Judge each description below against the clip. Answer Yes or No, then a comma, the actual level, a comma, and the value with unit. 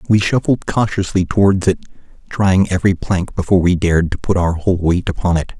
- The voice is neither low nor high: No, very low, 95 Hz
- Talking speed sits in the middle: Yes, average, 195 wpm